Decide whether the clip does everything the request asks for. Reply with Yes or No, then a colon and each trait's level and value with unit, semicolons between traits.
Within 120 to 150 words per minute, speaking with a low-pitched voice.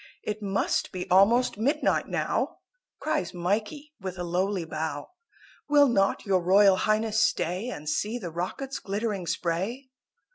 No: average, 140 wpm; high, 195 Hz